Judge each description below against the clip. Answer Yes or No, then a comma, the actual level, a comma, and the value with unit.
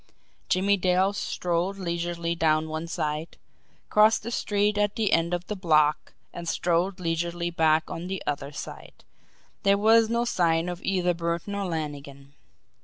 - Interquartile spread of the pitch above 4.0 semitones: No, average, 3.2 semitones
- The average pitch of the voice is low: No, medium, 175 Hz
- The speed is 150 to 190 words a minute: Yes, average, 155 wpm